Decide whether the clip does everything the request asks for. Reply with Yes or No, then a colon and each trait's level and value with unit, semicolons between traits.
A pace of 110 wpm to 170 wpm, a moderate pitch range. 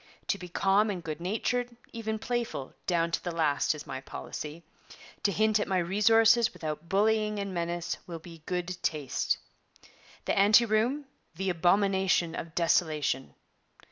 Yes: average, 150 wpm; average, 4.4 semitones